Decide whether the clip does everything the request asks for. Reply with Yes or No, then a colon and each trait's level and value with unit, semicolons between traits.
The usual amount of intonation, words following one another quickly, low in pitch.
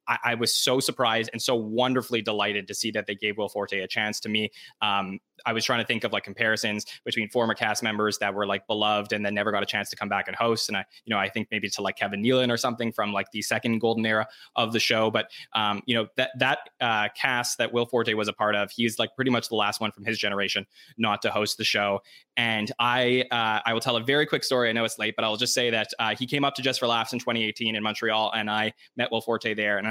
No: narrow, 2.1 semitones; fast, 275 wpm; low, 110 Hz